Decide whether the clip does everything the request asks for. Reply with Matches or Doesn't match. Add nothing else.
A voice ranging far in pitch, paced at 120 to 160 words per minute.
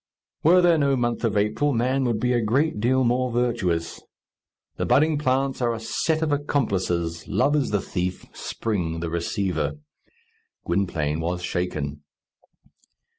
Matches